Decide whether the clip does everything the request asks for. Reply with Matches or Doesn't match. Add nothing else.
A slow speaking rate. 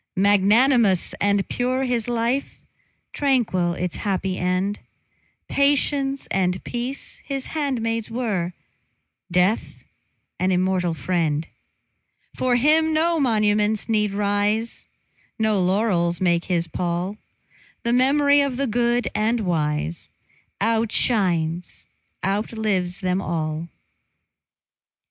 Matches